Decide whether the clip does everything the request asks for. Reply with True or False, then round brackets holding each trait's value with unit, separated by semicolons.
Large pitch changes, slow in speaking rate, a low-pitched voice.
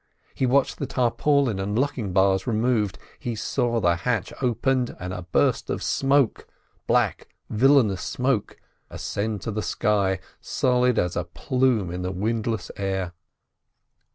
False (4.7 semitones; 130 wpm; 110 Hz)